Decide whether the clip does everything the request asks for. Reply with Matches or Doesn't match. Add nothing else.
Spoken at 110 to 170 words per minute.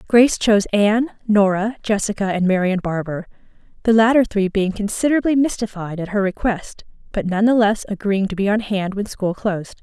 Matches